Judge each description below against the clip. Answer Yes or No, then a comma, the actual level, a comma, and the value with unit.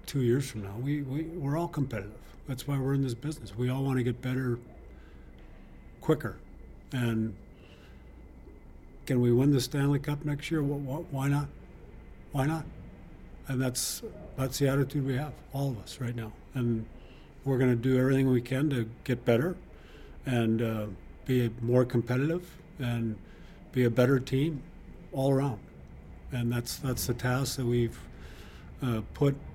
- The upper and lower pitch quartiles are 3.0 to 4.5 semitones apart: Yes, average, 3.8 semitones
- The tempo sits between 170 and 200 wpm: No, average, 160 wpm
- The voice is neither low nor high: No, low, 125 Hz